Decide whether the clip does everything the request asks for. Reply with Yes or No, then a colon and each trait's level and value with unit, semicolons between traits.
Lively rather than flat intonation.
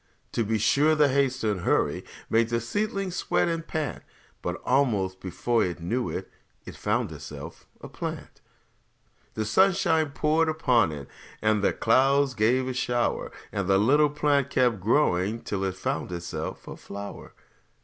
Yes: wide, 6.1 semitones